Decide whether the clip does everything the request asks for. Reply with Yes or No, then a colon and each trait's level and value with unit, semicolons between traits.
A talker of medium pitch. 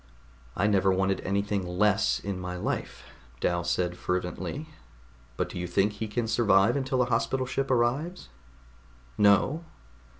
No: low, 100 Hz